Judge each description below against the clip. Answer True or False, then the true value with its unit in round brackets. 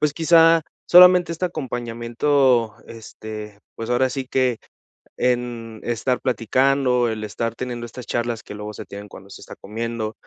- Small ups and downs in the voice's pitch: False (3.0 semitones)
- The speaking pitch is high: False (120 Hz)